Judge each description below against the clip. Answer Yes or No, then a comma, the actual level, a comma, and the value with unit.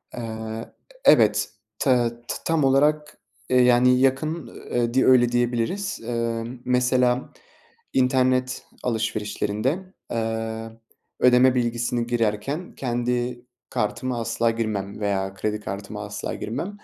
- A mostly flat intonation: Yes, narrow, 2.3 semitones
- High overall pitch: No, low, 120 Hz